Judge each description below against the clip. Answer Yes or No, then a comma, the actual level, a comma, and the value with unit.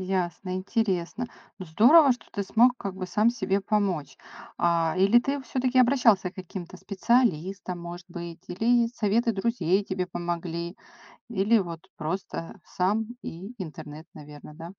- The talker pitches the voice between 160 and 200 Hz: Yes, high, 190 Hz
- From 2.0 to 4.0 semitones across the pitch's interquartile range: No, average, 4.7 semitones